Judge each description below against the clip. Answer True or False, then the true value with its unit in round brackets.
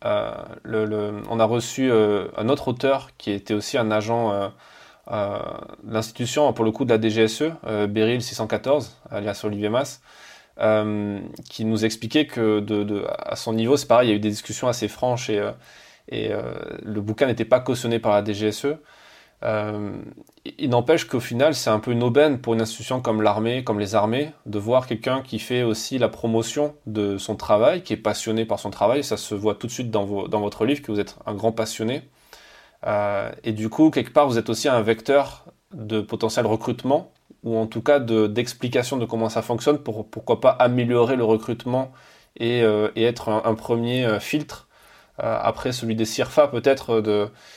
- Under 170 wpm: False (195 wpm)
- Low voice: True (115 Hz)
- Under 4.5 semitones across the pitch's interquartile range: True (2.9 semitones)